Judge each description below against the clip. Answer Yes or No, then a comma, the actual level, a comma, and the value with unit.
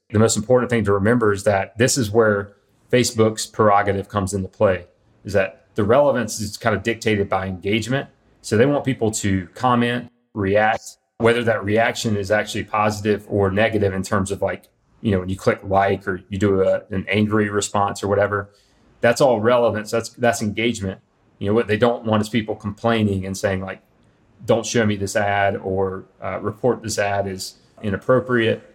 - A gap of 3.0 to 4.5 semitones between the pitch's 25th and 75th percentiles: No, narrow, 2.5 semitones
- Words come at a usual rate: Yes, average, 190 wpm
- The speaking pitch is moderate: No, low, 105 Hz